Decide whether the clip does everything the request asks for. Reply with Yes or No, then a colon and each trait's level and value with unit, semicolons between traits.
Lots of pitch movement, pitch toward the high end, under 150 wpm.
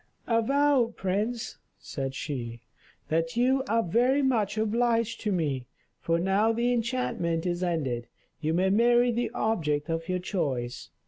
Yes: wide, 6.4 semitones; high, 200 Hz; average, 140 wpm